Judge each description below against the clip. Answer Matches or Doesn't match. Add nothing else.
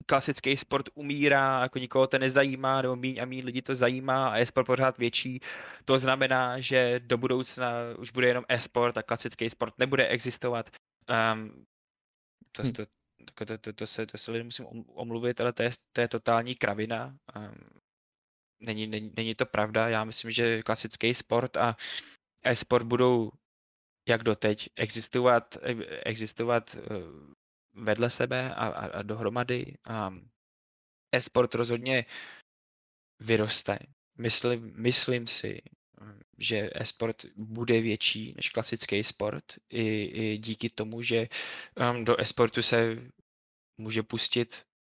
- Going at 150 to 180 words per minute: Doesn't match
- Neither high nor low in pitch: Doesn't match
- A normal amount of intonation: Doesn't match